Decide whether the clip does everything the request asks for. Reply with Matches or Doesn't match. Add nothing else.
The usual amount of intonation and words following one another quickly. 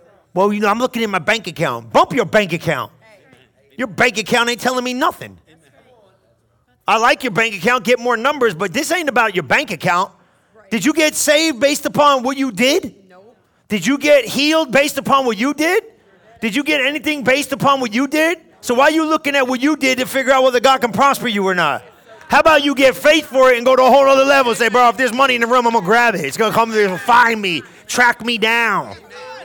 Matches